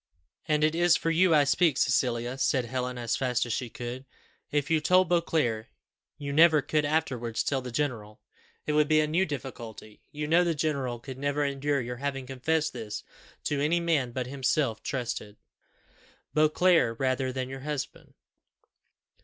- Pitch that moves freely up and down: No, average, 3.7 semitones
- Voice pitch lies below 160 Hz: Yes, medium, 140 Hz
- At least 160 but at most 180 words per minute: Yes, average, 170 wpm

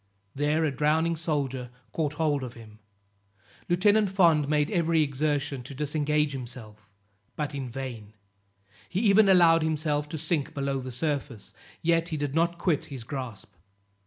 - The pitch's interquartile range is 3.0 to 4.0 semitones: Yes, average, 3.5 semitones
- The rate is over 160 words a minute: No, average, 150 wpm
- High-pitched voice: No, medium, 150 Hz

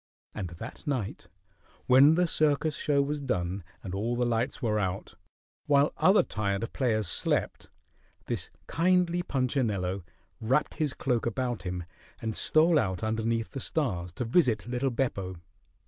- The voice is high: No, low, 120 Hz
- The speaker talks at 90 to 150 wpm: Yes, average, 145 wpm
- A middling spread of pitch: No, wide, 6.0 semitones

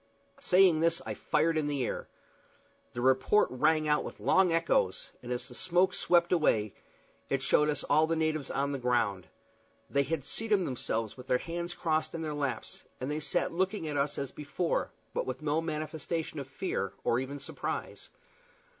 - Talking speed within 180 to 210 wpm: Yes, average, 185 wpm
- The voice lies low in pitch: No, medium, 150 Hz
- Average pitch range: Yes, average, 3.9 semitones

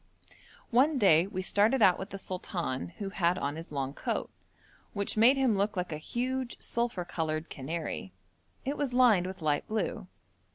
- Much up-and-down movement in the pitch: Yes, wide, 5.9 semitones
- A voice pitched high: Yes, high, 195 Hz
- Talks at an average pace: Yes, average, 170 wpm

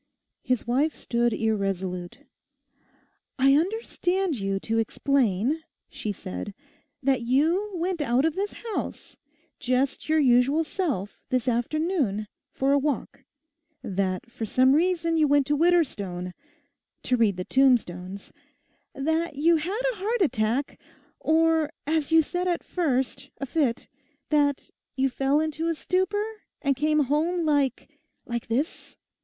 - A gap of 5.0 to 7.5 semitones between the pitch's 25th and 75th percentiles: Yes, wide, 5.4 semitones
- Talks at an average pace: No, slow, 130 wpm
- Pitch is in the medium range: No, very high, 280 Hz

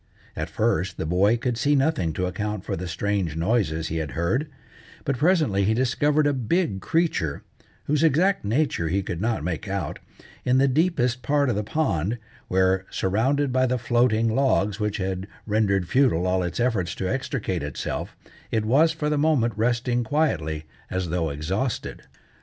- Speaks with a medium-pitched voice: No, low, 110 Hz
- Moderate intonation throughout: No, wide, 6.5 semitones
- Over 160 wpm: Yes, average, 170 wpm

